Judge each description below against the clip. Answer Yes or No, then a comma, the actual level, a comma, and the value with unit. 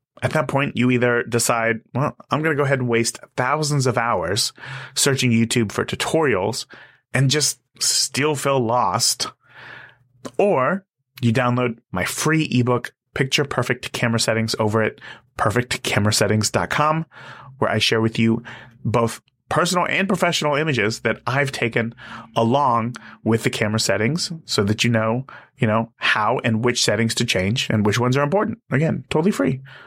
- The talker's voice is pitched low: Yes, low, 125 Hz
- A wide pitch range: No, average, 3.3 semitones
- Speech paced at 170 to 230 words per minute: No, average, 155 wpm